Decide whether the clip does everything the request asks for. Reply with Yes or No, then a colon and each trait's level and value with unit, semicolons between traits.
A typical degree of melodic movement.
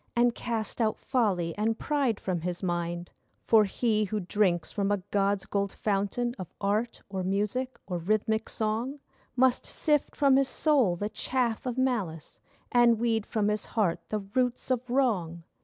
Yes: average, 3.9 semitones